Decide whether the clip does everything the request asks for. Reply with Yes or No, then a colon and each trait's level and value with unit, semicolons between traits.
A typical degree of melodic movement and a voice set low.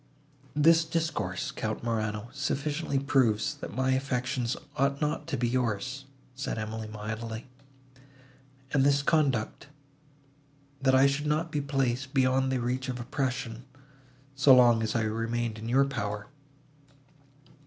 Yes: average, 3.4 semitones; low, 130 Hz